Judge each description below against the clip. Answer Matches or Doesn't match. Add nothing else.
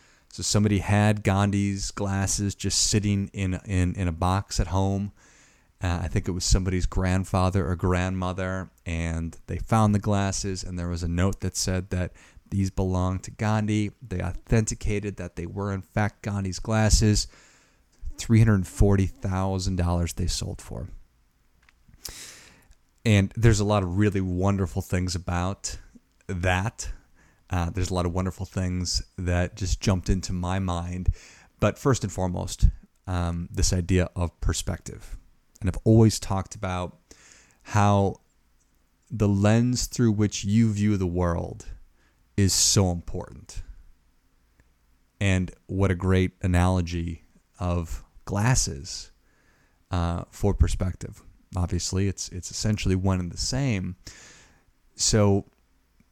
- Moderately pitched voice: Doesn't match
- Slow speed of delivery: Matches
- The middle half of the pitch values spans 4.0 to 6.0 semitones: Doesn't match